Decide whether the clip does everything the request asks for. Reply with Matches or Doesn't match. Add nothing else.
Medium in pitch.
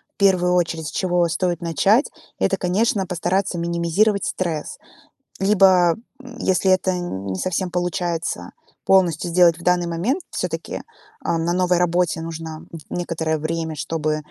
Matches